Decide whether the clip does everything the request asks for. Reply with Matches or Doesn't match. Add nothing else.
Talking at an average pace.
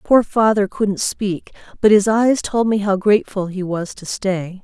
Matches